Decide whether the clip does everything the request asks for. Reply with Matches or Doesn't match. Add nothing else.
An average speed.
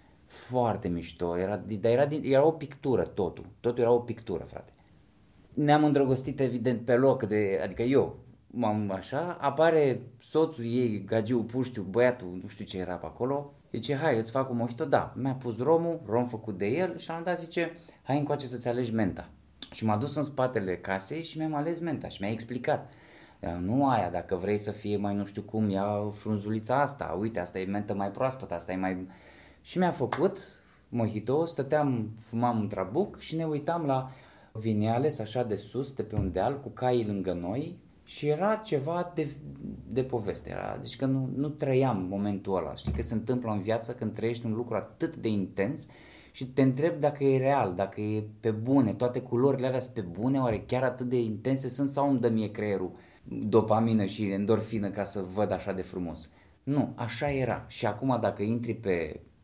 Doesn't match